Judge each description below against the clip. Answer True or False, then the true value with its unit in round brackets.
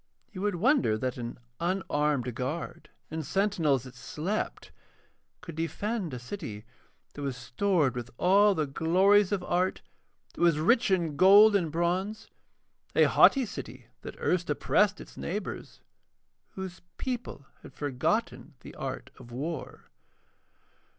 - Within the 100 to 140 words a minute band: True (135 wpm)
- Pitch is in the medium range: True (170 Hz)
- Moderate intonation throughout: False (6.1 semitones)